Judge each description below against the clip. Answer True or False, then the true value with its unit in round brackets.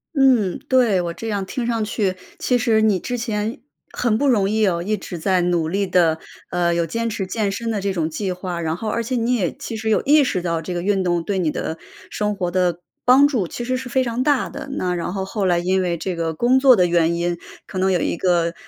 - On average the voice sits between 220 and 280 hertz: False (195 Hz)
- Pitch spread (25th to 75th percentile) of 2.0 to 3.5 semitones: False (4.8 semitones)